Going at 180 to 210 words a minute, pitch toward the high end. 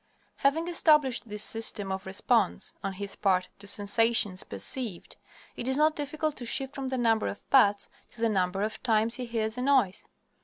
Yes: average, 185 wpm; high, 225 Hz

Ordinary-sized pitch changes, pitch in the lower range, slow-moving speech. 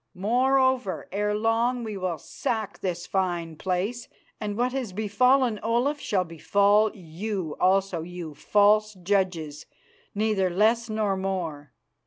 No: average, 3.7 semitones; high, 200 Hz; slow, 125 wpm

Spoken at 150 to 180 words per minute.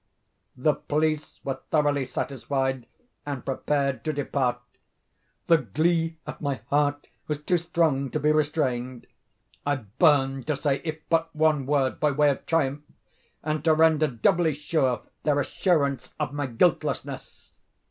No: average, 140 wpm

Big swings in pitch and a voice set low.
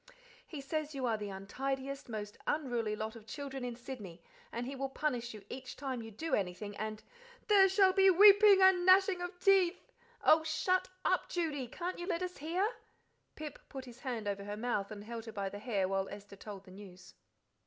No: wide, 8.7 semitones; very high, 260 Hz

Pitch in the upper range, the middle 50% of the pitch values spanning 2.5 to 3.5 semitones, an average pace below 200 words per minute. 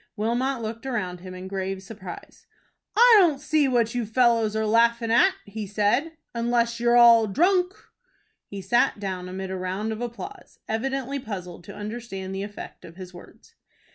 No: high, 225 Hz; average, 4.1 semitones; average, 170 wpm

